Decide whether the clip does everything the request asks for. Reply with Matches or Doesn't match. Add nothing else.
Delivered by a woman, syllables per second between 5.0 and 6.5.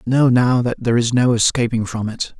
Doesn't match